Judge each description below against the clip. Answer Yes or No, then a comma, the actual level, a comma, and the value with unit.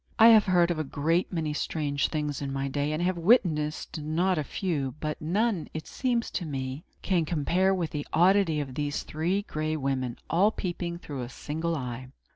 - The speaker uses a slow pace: No, average, 200 wpm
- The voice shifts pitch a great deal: No, average, 3.7 semitones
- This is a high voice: No, medium, 155 Hz